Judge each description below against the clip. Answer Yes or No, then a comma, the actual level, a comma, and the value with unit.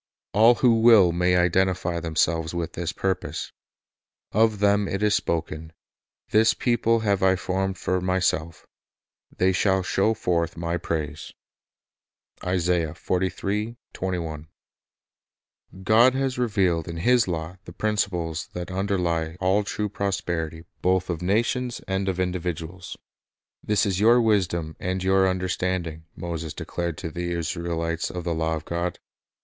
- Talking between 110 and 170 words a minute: Yes, slow, 135 wpm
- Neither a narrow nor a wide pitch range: Yes, average, 3.1 semitones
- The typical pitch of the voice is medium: No, very low, 90 Hz